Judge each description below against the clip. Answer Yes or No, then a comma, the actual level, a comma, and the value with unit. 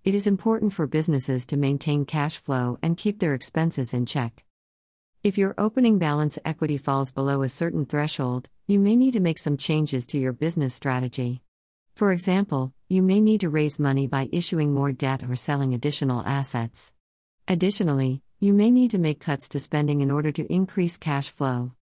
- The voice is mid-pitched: Yes, medium, 145 Hz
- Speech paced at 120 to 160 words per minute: No, average, 185 wpm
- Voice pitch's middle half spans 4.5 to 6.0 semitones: Yes, average, 5.0 semitones